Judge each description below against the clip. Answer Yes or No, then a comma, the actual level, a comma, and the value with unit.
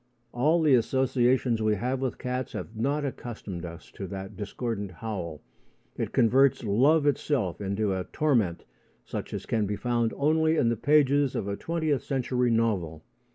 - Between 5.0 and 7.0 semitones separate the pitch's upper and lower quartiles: Yes, average, 5.3 semitones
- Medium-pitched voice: No, low, 120 Hz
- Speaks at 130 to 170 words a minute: Yes, average, 160 wpm